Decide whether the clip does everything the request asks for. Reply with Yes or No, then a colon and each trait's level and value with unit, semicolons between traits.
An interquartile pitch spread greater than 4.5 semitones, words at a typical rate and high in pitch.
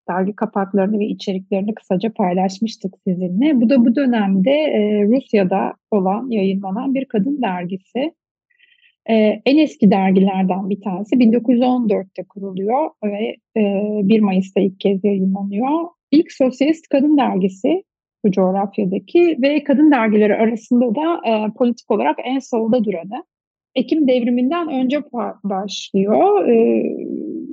Yes: average, 5.2 semitones; average, 120 wpm; high, 225 Hz